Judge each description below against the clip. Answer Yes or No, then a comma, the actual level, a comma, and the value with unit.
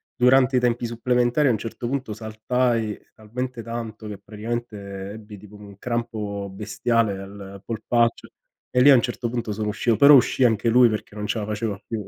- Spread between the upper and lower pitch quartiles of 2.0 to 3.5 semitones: Yes, narrow, 2.5 semitones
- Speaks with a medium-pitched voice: No, low, 115 Hz